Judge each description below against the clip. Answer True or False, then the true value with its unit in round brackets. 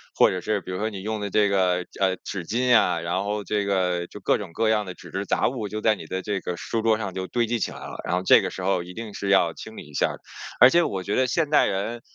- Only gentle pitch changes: False (3.0 semitones)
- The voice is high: False (100 Hz)